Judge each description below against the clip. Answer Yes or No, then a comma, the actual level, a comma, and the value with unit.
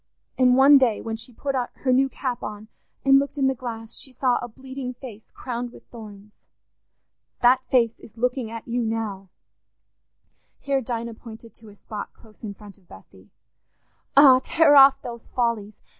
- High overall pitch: Yes, high, 240 Hz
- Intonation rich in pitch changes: No, average, 3.1 semitones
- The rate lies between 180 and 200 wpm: No, average, 165 wpm